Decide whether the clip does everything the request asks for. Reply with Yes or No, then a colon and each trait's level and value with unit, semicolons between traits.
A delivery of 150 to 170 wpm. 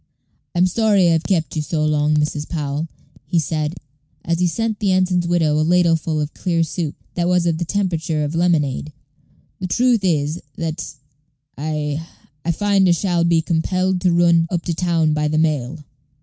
No: average, 180 wpm